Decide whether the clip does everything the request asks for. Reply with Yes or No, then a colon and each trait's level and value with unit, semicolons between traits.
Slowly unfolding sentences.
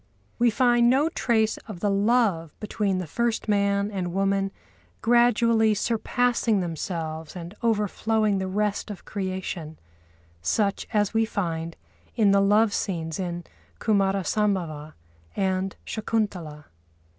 Yes: slow, 120 wpm